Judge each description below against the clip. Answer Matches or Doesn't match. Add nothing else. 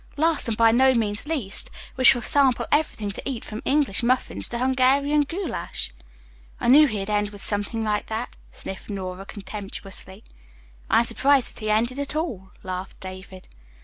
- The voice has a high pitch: Matches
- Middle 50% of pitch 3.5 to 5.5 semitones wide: Matches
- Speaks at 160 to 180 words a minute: Matches